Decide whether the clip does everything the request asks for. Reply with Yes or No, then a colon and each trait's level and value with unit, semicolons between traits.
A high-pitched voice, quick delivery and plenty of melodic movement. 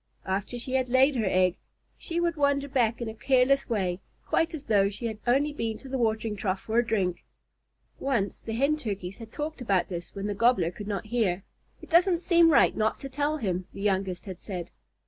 Yes: high, 225 Hz; fast, 215 wpm; wide, 5.7 semitones